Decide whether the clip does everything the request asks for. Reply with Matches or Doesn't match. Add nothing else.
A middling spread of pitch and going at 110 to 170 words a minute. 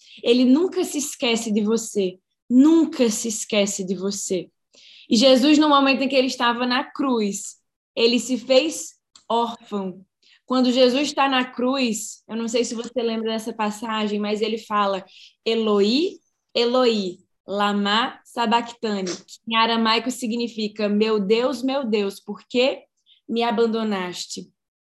Matches